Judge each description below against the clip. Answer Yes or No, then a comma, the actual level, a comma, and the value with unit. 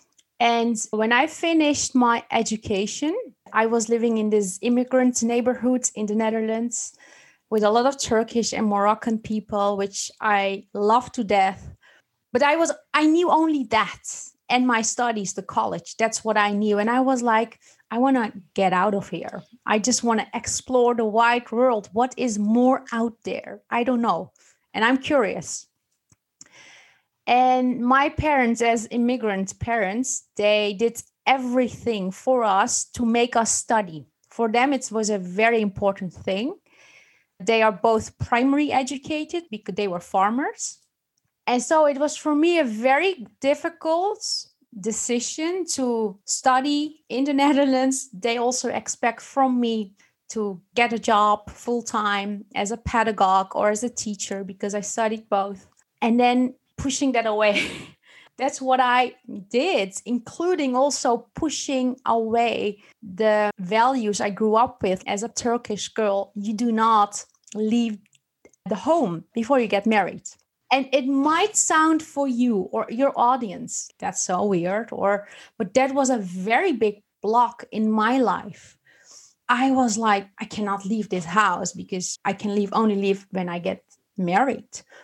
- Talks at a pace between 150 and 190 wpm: Yes, average, 155 wpm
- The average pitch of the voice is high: Yes, high, 230 Hz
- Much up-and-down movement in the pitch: No, average, 3.6 semitones